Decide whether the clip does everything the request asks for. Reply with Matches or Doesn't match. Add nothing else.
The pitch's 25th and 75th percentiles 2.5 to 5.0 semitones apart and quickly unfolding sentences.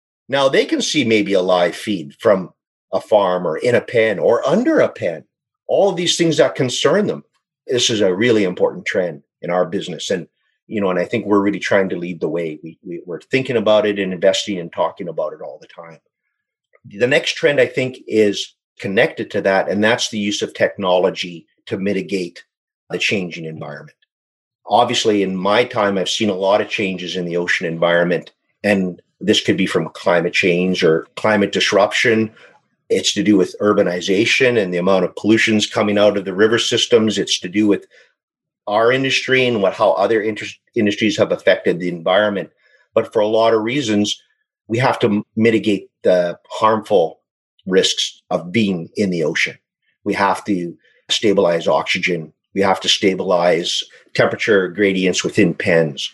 Doesn't match